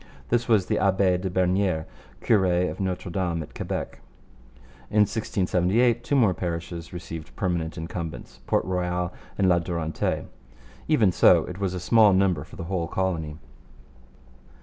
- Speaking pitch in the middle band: No, very low, 90 Hz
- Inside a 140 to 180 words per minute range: Yes, average, 150 wpm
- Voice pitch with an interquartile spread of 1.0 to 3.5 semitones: Yes, narrow, 2.4 semitones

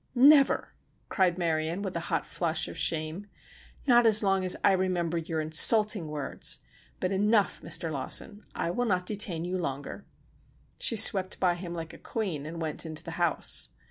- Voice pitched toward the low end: No, medium, 180 Hz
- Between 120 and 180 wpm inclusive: Yes, average, 175 wpm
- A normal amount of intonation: Yes, average, 4.0 semitones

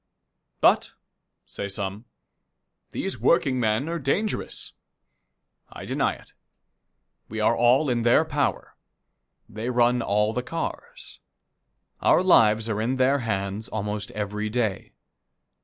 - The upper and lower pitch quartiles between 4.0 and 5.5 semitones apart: No, average, 3.5 semitones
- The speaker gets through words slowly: Yes, slow, 115 wpm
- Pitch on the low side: Yes, low, 115 Hz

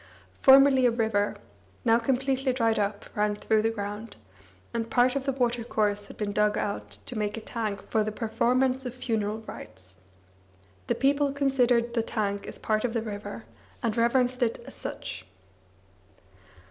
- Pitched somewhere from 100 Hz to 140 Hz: No, high, 230 Hz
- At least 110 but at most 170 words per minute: Yes, average, 160 wpm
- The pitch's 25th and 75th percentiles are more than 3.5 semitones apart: No, average, 3.1 semitones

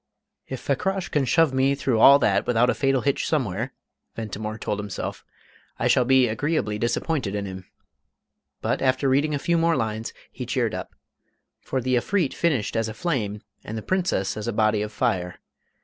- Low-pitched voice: Yes, low, 125 Hz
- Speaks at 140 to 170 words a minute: No, average, 180 wpm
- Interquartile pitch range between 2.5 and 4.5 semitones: No, average, 4.9 semitones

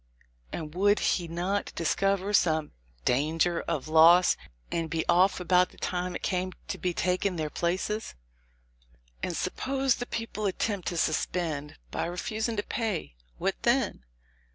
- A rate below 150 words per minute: Yes, average, 140 wpm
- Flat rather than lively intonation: No, average, 3.4 semitones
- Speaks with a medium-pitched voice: Yes, medium, 180 Hz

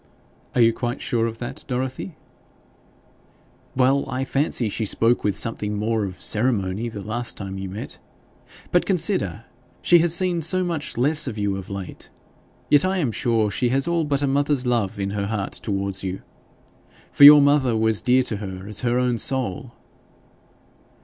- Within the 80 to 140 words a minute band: No, average, 175 wpm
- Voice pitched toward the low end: Yes, low, 120 Hz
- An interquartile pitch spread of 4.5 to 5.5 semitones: Yes, average, 5.2 semitones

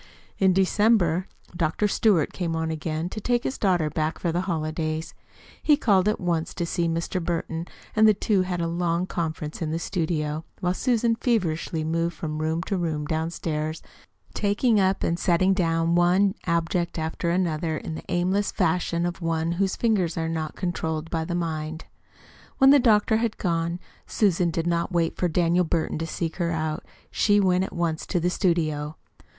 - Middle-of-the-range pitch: Yes, medium, 170 Hz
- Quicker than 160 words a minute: Yes, average, 180 wpm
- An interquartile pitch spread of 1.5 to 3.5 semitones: Yes, narrow, 2.5 semitones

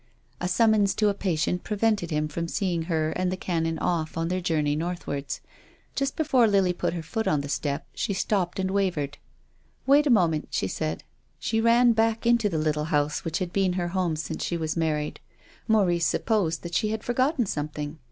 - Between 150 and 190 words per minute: No, average, 200 wpm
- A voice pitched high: No, medium, 180 Hz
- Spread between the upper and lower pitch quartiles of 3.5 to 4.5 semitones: No, average, 5.1 semitones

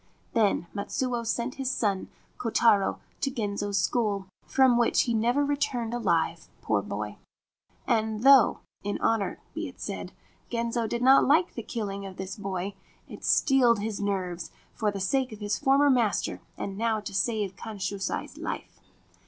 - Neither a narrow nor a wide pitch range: Yes, average, 3.6 semitones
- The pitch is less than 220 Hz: No, high, 225 Hz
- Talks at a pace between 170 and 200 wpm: No, average, 155 wpm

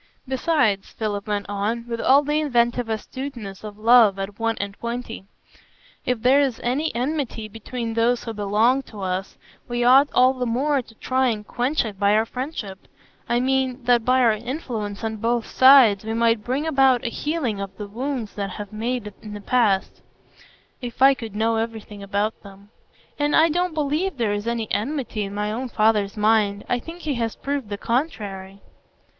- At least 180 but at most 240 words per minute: Yes, average, 185 wpm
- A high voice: Yes, high, 230 Hz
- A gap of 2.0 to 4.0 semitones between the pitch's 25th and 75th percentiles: Yes, average, 3.7 semitones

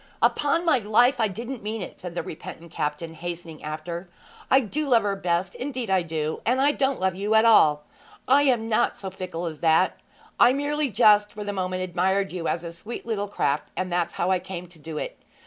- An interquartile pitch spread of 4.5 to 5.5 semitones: Yes, average, 5.2 semitones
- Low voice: No, high, 190 Hz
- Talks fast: Yes, fast, 215 wpm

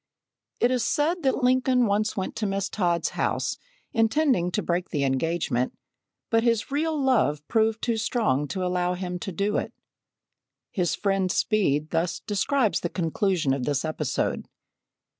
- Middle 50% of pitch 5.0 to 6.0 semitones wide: Yes, wide, 5.5 semitones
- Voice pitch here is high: Yes, high, 195 Hz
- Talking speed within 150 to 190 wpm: Yes, average, 155 wpm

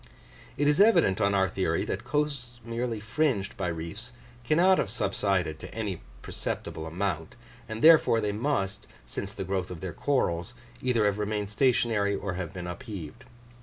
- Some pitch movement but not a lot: Yes, average, 4.5 semitones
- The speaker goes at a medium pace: Yes, average, 165 wpm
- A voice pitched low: Yes, low, 105 Hz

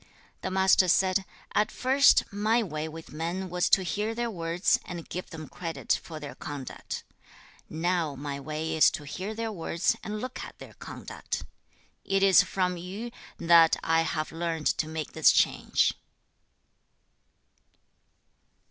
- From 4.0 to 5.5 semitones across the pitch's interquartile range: No, average, 3.5 semitones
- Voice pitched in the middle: Yes, medium, 175 Hz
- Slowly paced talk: No, average, 150 wpm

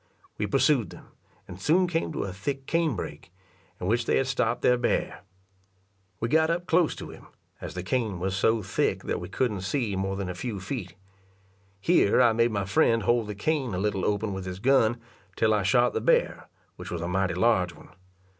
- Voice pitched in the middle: No, low, 110 Hz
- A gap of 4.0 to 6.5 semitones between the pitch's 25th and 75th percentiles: Yes, average, 4.9 semitones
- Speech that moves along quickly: Yes, fast, 210 wpm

